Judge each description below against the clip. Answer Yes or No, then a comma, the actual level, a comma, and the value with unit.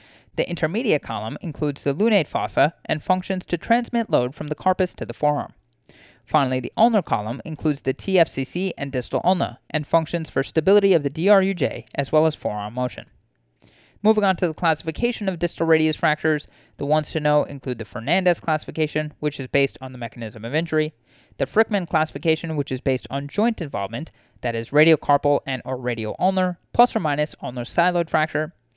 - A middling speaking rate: Yes, average, 180 wpm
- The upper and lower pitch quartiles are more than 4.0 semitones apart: Yes, average, 4.9 semitones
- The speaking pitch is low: No, medium, 155 Hz